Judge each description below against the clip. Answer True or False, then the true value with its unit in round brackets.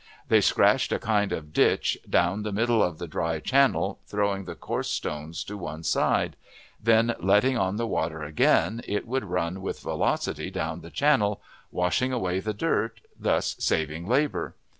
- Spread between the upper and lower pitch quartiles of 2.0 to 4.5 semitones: False (5.3 semitones)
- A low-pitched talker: True (100 Hz)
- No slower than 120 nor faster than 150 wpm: False (165 wpm)